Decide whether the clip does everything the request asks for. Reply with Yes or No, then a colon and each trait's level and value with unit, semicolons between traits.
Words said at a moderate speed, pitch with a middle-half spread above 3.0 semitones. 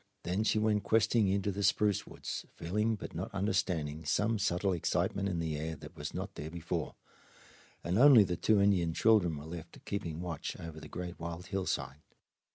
Yes: average, 180 wpm; average, 3.9 semitones